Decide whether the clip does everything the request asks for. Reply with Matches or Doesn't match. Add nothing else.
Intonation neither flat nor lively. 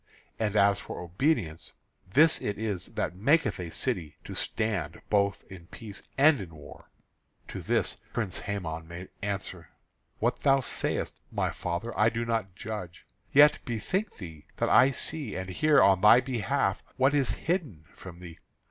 Doesn't match